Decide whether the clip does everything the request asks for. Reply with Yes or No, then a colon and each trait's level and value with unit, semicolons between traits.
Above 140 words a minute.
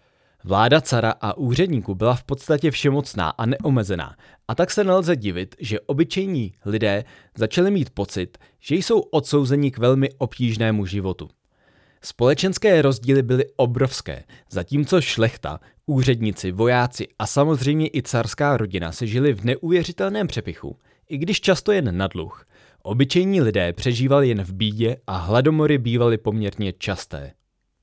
No: average, 135 wpm